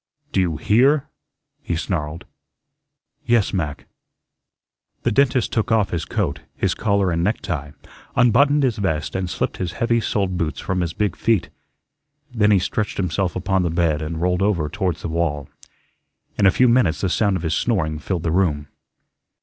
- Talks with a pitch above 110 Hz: No, very low, 95 Hz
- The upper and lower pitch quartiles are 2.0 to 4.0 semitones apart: No, average, 4.4 semitones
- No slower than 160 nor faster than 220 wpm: Yes, average, 170 wpm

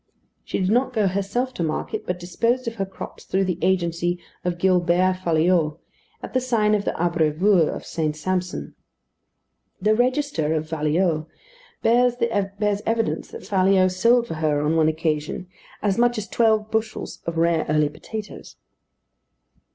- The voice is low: No, medium, 185 Hz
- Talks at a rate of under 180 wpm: Yes, average, 150 wpm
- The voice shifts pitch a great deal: No, average, 4.7 semitones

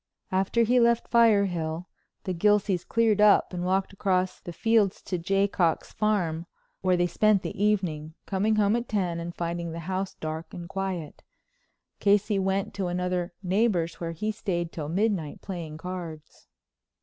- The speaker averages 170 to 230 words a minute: No, average, 160 wpm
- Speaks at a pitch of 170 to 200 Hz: Yes, medium, 185 Hz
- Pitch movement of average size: Yes, average, 3.3 semitones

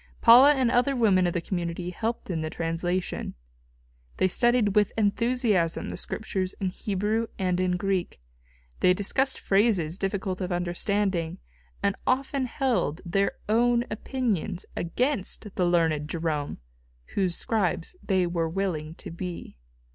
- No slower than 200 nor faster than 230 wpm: No, slow, 135 wpm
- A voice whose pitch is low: No, high, 190 Hz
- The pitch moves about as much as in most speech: Yes, average, 4.5 semitones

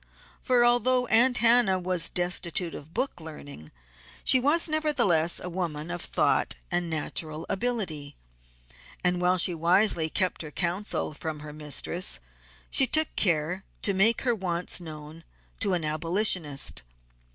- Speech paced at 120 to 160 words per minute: Yes, average, 140 wpm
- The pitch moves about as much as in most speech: No, wide, 5.8 semitones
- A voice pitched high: No, medium, 180 Hz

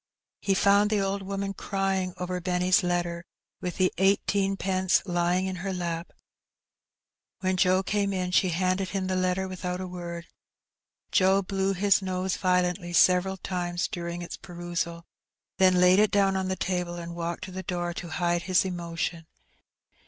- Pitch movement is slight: Yes, narrow, 1.6 semitones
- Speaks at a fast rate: No, average, 160 wpm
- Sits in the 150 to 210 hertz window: Yes, medium, 185 Hz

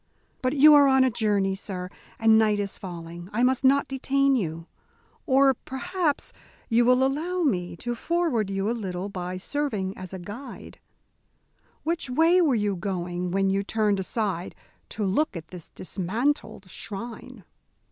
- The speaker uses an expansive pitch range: Yes, wide, 6.1 semitones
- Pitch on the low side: No, high, 220 Hz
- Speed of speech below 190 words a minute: Yes, average, 155 wpm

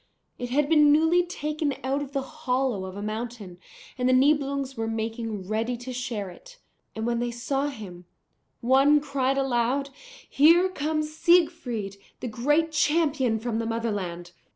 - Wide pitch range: No, average, 4.7 semitones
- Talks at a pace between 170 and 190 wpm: No, average, 155 wpm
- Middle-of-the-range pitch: No, very high, 260 Hz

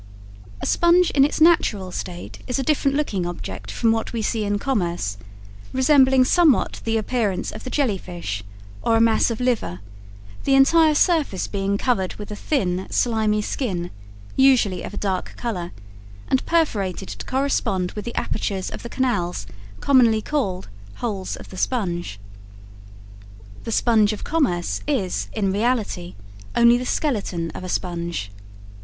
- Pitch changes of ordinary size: No, wide, 6.0 semitones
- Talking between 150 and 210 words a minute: Yes, average, 155 wpm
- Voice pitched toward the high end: Yes, high, 220 Hz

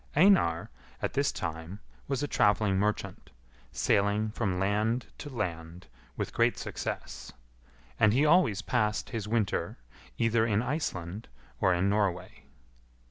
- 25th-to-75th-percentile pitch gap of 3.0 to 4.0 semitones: Yes, average, 3.6 semitones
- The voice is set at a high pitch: No, low, 105 Hz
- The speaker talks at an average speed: No, slow, 130 wpm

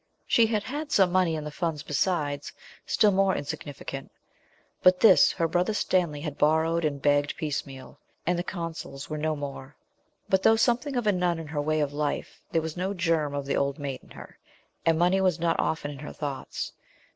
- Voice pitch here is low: No, medium, 160 Hz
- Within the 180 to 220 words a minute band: Yes, average, 200 wpm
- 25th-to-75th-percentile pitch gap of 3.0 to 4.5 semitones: Yes, average, 4.0 semitones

